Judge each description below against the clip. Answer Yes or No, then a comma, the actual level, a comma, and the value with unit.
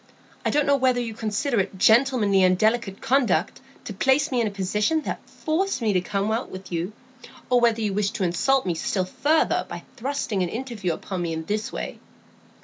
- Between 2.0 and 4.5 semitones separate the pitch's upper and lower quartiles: No, average, 5.3 semitones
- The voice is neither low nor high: No, high, 215 Hz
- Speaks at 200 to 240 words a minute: Yes, fast, 205 wpm